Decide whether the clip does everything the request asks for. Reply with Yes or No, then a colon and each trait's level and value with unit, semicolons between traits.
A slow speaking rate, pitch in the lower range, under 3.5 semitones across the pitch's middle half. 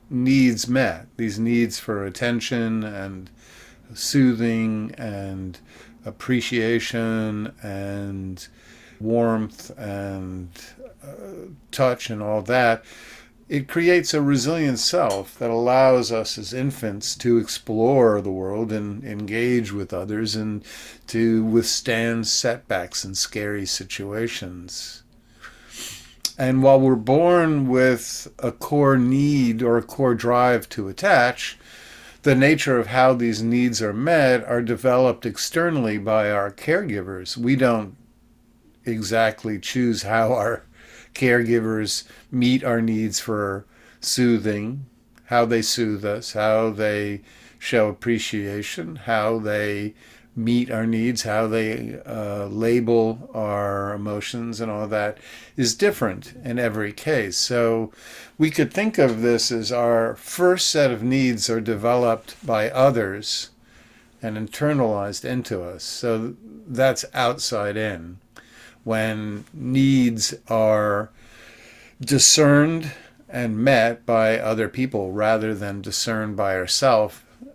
Yes: slow, 115 wpm; low, 115 Hz; average, 2.8 semitones